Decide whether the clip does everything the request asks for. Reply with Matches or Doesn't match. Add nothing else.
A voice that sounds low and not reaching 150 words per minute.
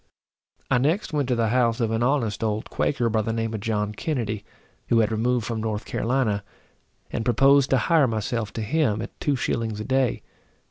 Doesn't match